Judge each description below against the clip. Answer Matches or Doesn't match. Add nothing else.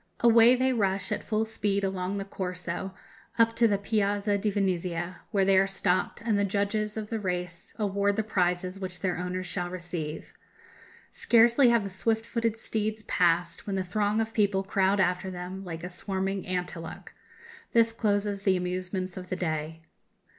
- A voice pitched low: Doesn't match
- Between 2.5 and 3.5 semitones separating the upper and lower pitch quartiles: Matches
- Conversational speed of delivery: Matches